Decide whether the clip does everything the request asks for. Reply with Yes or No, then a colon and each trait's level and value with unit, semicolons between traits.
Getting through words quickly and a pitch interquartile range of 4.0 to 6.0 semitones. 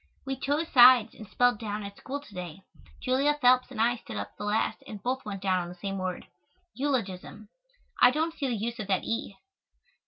Yes: fast, 210 wpm; average, 4.7 semitones